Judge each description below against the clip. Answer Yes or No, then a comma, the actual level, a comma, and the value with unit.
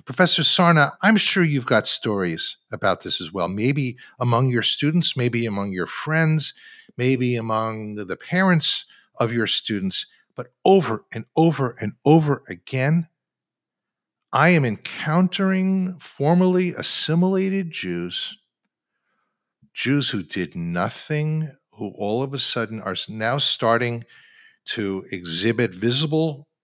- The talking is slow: Yes, slow, 120 wpm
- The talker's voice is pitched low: Yes, low, 130 Hz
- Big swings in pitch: Yes, wide, 6.9 semitones